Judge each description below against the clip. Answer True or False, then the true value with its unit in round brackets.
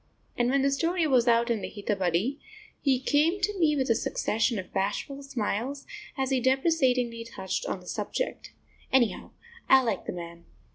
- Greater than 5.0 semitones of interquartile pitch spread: False (4.1 semitones)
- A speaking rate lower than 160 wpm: False (175 wpm)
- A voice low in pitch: False (255 Hz)